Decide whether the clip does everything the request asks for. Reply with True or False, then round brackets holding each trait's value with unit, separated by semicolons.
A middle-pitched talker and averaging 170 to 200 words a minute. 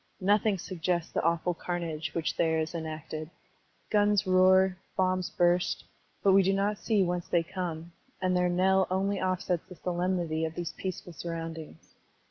False (180 Hz; 155 wpm)